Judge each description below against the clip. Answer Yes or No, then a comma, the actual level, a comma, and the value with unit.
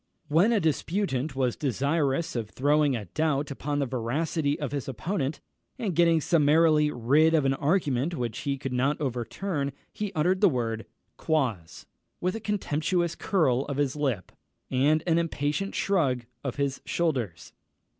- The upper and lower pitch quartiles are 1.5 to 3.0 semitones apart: No, average, 4.0 semitones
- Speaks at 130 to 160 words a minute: Yes, average, 155 wpm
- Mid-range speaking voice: Yes, medium, 145 Hz